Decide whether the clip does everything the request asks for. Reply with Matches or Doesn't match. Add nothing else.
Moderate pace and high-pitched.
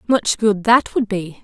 Doesn't match